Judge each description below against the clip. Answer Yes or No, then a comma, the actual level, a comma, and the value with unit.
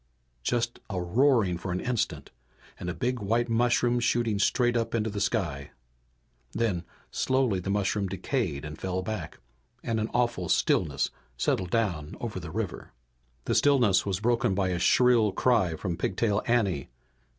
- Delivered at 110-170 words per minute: Yes, average, 155 wpm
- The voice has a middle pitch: No, low, 105 Hz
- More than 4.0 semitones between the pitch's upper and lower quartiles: Yes, average, 4.7 semitones